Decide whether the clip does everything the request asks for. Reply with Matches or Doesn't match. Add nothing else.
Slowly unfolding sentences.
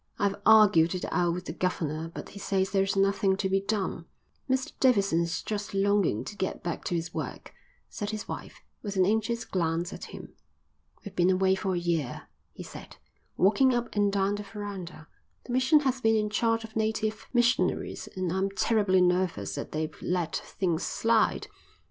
Doesn't match